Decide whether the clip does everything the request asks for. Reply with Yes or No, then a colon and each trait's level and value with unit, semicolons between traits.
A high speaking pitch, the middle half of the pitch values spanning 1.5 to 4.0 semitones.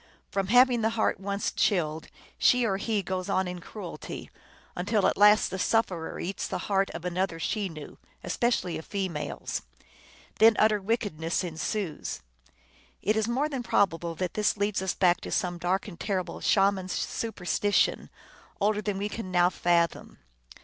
Yes: high, 195 Hz; average, 3.2 semitones